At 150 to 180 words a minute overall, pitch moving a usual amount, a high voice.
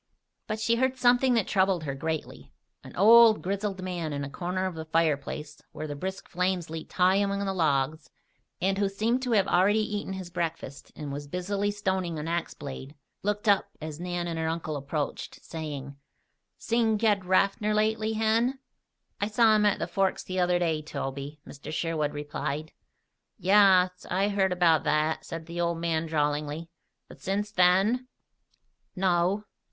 No: average, 170 wpm; average, 4.5 semitones; medium, 180 Hz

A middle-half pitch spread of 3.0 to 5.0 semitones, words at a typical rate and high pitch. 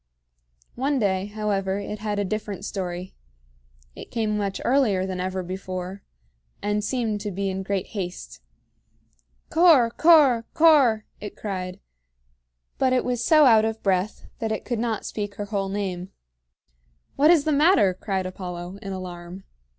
Yes: average, 3.5 semitones; average, 150 wpm; high, 205 Hz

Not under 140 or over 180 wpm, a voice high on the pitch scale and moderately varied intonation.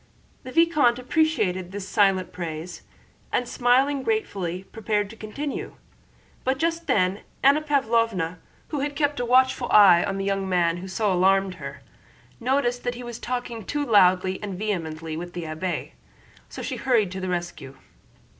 No: average, 160 wpm; high, 205 Hz; wide, 5.8 semitones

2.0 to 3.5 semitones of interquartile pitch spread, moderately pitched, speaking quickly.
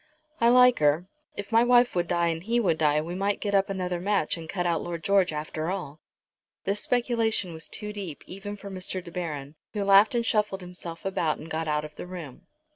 No: average, 3.9 semitones; medium, 180 Hz; fast, 220 wpm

